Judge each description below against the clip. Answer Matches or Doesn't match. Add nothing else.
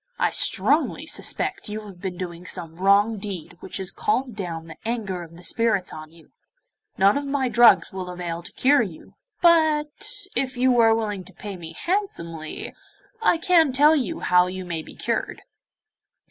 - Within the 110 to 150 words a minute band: Doesn't match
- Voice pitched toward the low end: Doesn't match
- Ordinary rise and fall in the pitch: Doesn't match